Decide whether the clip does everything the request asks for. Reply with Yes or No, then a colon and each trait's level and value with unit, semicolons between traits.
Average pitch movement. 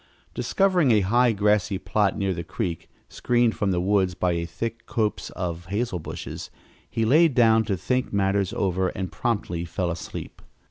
Yes: average, 4.1 semitones